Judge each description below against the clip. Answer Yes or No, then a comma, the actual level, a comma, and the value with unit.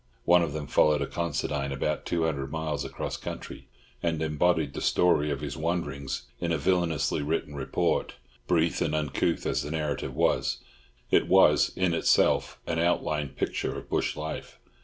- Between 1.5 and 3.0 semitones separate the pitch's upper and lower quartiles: Yes, average, 2.7 semitones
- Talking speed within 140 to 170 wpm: Yes, average, 165 wpm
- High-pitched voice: No, very low, 75 Hz